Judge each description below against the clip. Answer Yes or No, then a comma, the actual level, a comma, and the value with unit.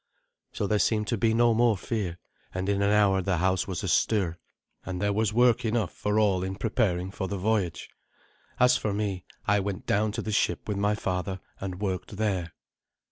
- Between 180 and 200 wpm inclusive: Yes, average, 195 wpm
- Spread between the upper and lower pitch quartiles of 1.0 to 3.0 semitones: Yes, narrow, 2.5 semitones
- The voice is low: Yes, low, 100 Hz